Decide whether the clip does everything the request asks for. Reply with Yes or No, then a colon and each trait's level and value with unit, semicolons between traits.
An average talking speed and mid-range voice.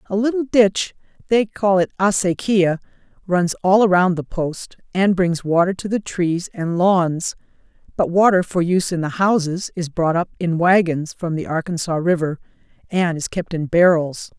Yes: average, 165 wpm; medium, 180 Hz